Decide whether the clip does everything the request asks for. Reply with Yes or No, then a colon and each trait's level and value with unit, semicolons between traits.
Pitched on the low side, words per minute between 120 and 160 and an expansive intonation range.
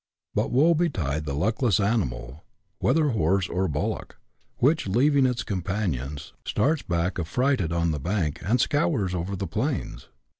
Yes: low, 100 Hz; average, 150 wpm; wide, 7.4 semitones